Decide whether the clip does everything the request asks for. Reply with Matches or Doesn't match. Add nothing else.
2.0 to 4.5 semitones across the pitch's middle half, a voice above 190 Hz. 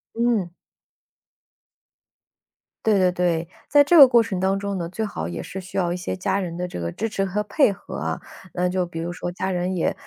Doesn't match